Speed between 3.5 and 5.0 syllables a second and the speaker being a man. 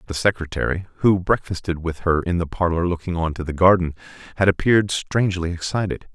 No: 5.9 syllables/s; male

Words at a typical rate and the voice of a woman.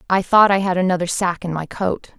No: fast, 245 wpm; female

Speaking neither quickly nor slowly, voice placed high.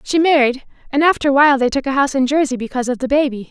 No: fast, 275 wpm; very high, 270 Hz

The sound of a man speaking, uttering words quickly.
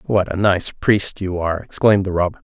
Yes: male; fast, 215 wpm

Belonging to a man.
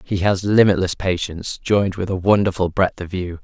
Yes: male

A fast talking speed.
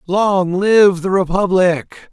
No: slow, 115 wpm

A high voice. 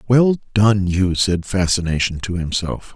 No: very low, 95 Hz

